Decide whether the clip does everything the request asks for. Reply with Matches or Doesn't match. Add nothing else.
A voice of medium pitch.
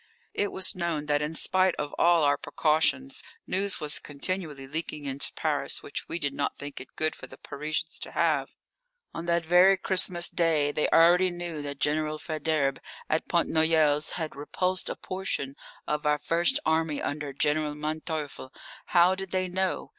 Matches